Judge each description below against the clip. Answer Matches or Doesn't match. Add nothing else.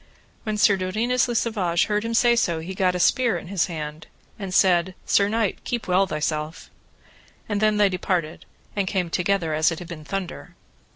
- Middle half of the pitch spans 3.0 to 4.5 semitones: Matches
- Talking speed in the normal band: Matches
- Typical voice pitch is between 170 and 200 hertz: Matches